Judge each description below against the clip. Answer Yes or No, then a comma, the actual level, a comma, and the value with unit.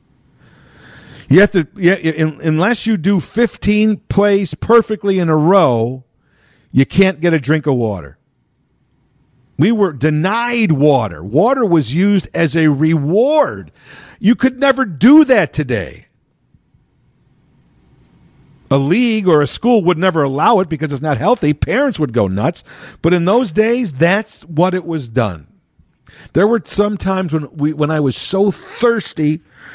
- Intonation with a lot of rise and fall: Yes, wide, 6.0 semitones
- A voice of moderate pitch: Yes, medium, 170 Hz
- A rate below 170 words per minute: Yes, average, 145 wpm